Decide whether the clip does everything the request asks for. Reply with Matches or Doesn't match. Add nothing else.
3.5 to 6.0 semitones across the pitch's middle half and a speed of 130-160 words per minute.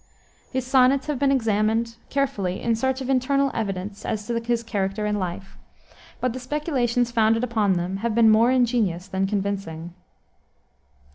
Matches